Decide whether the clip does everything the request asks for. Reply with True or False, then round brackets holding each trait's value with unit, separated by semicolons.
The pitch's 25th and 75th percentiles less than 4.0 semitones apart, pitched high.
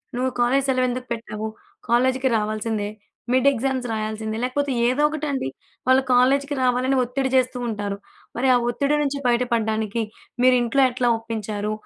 True (3.1 semitones; 250 Hz)